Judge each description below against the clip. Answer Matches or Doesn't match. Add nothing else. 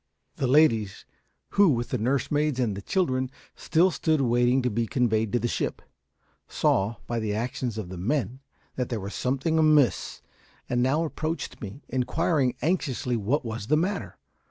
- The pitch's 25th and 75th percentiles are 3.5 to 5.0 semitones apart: Matches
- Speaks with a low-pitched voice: Matches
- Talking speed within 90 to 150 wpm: Doesn't match